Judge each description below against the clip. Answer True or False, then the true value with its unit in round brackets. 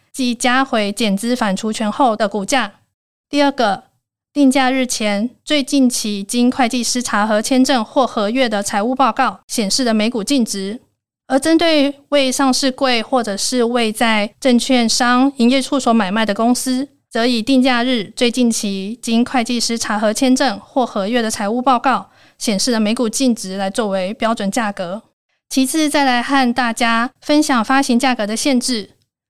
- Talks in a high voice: True (245 Hz)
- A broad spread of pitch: False (3.2 semitones)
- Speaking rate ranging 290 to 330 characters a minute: False (250 characters per minute)